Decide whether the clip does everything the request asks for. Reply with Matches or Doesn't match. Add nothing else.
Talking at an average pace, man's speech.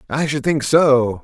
Matches